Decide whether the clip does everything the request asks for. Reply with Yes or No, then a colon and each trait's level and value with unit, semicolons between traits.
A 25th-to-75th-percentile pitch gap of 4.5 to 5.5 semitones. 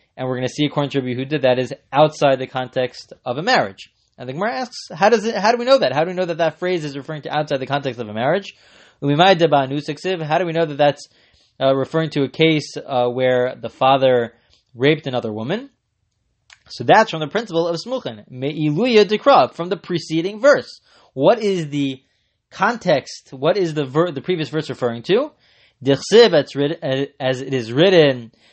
Yes: average, 5.1 semitones